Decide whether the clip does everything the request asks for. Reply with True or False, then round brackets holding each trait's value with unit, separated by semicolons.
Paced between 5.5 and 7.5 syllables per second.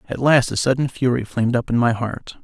True (5.7 syllables/s)